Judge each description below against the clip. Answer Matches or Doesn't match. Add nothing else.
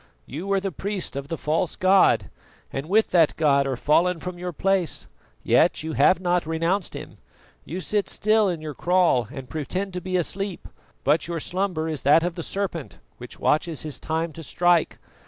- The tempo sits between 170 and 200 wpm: Matches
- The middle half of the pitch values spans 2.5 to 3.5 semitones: Matches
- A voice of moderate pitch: Matches